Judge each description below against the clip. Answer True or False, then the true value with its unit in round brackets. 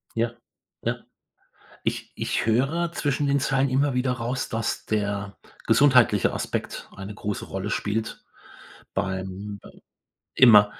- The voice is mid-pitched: False (115 Hz)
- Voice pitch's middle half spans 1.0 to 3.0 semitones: False (4.6 semitones)